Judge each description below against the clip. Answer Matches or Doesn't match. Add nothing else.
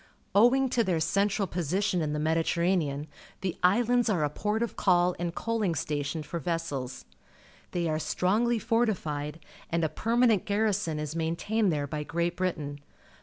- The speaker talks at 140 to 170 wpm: Matches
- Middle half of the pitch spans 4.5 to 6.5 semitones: Matches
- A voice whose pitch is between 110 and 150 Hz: Doesn't match